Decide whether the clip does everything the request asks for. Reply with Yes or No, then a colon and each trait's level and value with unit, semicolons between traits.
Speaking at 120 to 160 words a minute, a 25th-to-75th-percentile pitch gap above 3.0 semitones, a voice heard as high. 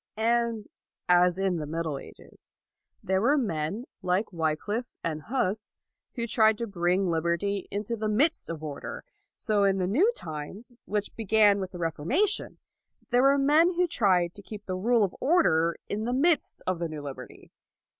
No: average, 170 wpm; average, 5.3 semitones; high, 200 Hz